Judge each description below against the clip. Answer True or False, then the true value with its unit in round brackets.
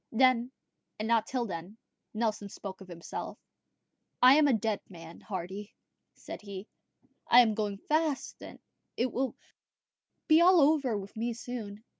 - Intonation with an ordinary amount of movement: True (4.2 semitones)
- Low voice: False (220 Hz)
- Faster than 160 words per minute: False (145 wpm)